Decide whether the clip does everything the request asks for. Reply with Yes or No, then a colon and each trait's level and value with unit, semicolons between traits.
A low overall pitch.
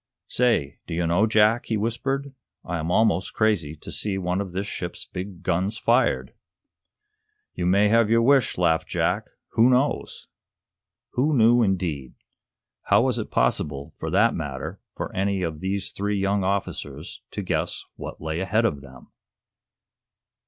Yes: low, 100 Hz